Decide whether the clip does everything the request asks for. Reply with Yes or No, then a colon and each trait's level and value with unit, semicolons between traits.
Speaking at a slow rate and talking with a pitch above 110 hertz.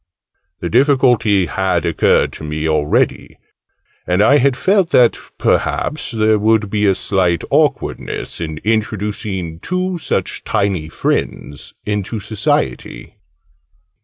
No: slow, 115 wpm; low, 105 Hz